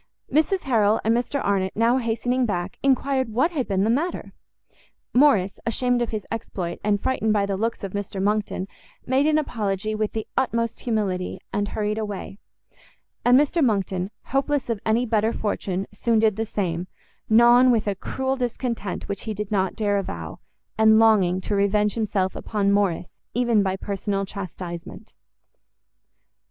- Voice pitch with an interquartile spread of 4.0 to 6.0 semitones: No, average, 3.4 semitones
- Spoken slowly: No, average, 160 wpm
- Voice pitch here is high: Yes, high, 215 Hz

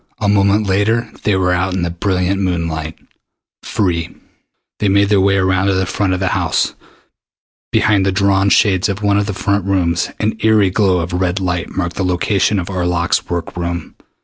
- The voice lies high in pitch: No, very low, 95 Hz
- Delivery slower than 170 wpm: No, average, 195 wpm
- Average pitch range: No, narrow, 2.1 semitones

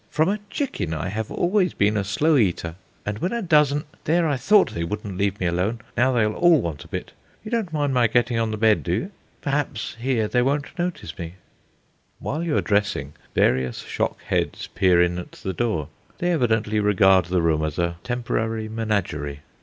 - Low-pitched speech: Yes, low, 110 Hz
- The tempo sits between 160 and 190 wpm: No, average, 200 wpm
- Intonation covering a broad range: Yes, wide, 8.0 semitones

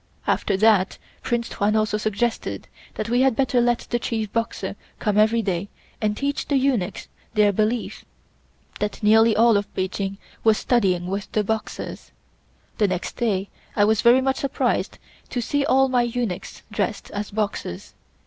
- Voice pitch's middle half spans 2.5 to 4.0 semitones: Yes, average, 2.8 semitones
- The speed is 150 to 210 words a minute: Yes, average, 160 wpm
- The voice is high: Yes, high, 220 Hz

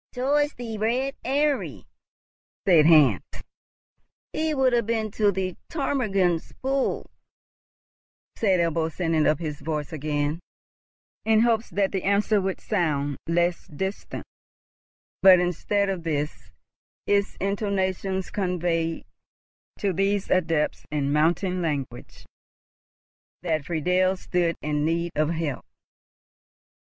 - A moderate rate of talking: No, slow, 110 wpm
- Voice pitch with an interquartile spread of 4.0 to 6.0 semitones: Yes, average, 4.4 semitones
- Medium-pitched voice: Yes, medium, 180 Hz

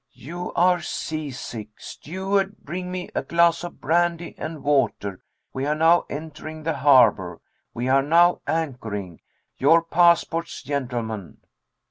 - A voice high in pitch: No, medium, 155 Hz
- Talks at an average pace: No, slow, 125 wpm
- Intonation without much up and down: No, average, 4.7 semitones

